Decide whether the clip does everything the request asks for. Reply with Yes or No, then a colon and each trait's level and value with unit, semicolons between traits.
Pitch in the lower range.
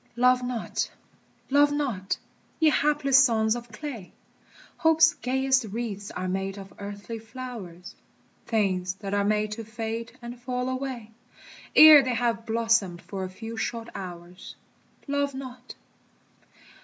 No: high, 230 Hz